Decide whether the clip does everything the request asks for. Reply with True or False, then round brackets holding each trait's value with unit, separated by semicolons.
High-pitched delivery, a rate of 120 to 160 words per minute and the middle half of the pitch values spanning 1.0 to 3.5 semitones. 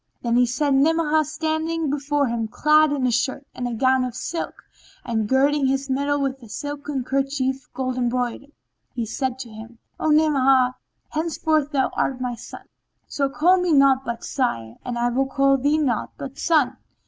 False (270 Hz; 170 wpm; 2.9 semitones)